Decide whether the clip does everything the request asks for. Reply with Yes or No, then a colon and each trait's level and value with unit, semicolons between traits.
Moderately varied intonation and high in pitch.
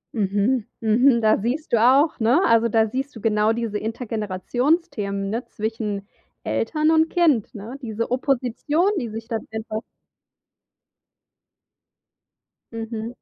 Yes: average, 3.3 semitones; high, 230 Hz